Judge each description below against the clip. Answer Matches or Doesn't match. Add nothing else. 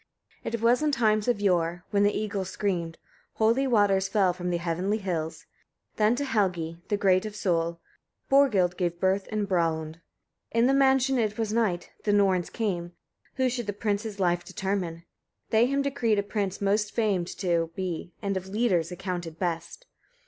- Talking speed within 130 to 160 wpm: Doesn't match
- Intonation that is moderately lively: Matches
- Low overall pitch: Doesn't match